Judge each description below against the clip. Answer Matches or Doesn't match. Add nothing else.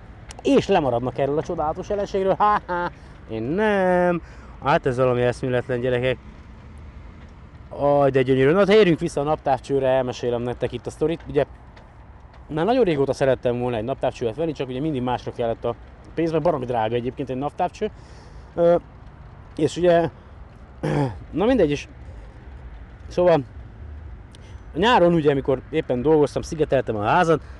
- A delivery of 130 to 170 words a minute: Matches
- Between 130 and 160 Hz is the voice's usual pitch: Matches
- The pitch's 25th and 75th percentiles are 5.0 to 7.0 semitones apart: Matches